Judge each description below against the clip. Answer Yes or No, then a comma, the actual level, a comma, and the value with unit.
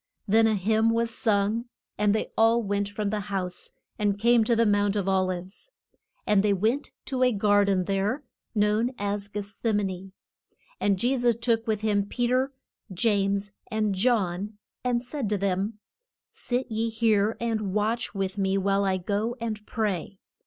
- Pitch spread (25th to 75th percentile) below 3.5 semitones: Yes, narrow, 2.4 semitones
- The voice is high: Yes, high, 210 Hz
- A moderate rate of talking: Yes, average, 180 wpm